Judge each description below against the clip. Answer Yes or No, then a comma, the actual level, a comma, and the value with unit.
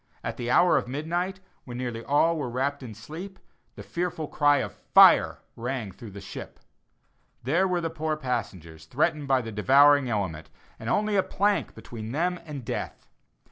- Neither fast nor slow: Yes, average, 175 wpm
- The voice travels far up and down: Yes, wide, 5.8 semitones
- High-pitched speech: No, medium, 140 Hz